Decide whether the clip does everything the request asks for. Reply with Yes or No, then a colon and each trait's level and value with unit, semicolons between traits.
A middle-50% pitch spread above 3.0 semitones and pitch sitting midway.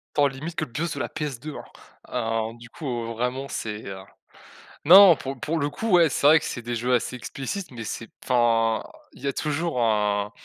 No: average, 4.8 semitones; low, 125 Hz